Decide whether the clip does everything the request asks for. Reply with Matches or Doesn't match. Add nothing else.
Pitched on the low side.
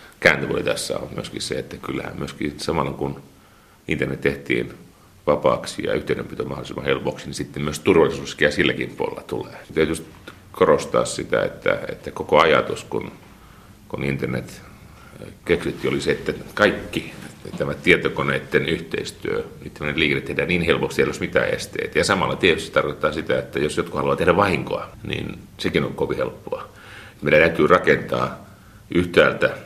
Matches